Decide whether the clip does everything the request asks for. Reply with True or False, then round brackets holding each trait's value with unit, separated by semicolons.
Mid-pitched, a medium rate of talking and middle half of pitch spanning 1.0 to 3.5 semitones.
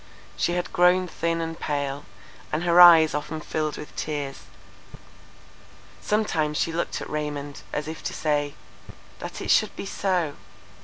True (155 Hz; 145 wpm; 2.6 semitones)